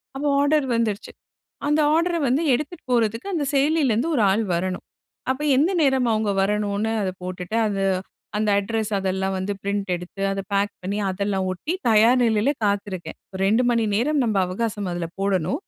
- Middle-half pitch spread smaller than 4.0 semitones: No, average, 5.0 semitones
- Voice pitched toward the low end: No, high, 215 Hz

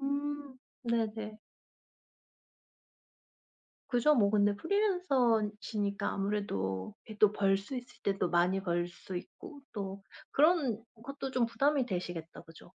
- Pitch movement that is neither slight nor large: No, wide, 5.7 semitones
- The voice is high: Yes, high, 215 Hz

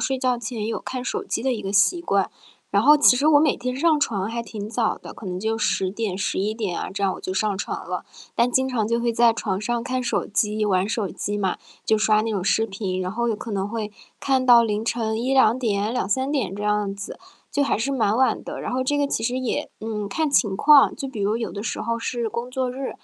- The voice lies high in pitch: Yes, high, 225 Hz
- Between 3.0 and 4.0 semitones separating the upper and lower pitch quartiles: Yes, average, 3.6 semitones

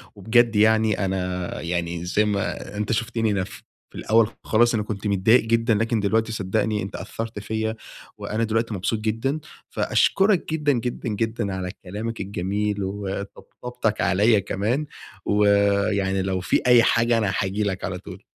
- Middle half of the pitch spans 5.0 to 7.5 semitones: No, narrow, 2.5 semitones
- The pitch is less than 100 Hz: No, low, 105 Hz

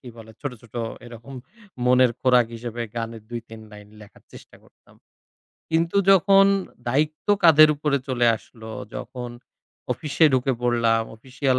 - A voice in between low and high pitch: No, low, 125 Hz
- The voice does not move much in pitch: No, average, 3.9 semitones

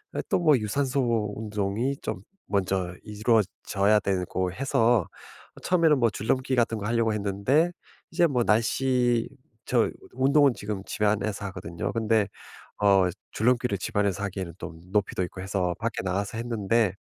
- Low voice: Yes, low, 110 Hz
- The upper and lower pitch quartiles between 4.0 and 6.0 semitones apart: No, average, 3.5 semitones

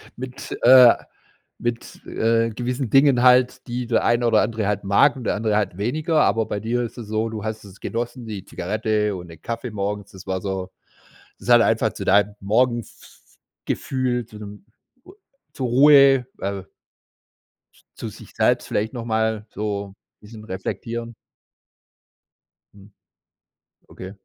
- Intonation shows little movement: No, average, 3.0 semitones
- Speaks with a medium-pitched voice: No, low, 110 Hz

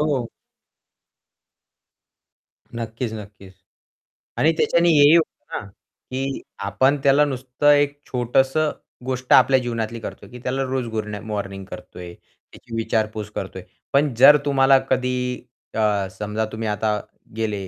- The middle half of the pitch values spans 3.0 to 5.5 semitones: Yes, average, 4.0 semitones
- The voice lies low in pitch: Yes, low, 125 Hz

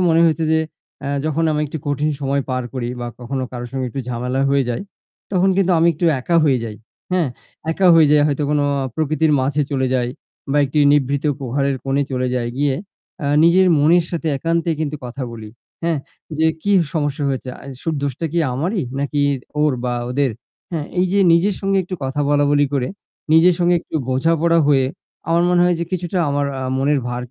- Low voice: No, medium, 145 Hz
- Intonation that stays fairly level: No, average, 3.8 semitones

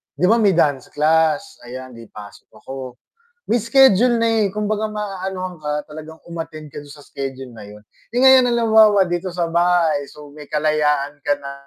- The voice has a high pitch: No, medium, 160 Hz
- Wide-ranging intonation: Yes, wide, 6.1 semitones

